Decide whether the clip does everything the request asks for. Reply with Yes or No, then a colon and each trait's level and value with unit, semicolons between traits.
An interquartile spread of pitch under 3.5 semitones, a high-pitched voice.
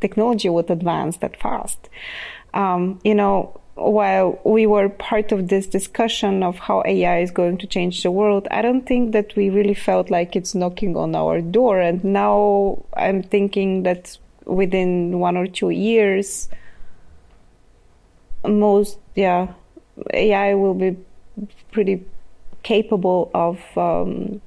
Yes: average, 2.7 semitones; high, 195 Hz